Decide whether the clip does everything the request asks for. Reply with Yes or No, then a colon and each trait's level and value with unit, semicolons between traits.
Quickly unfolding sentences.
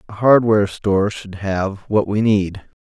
No: average, 170 wpm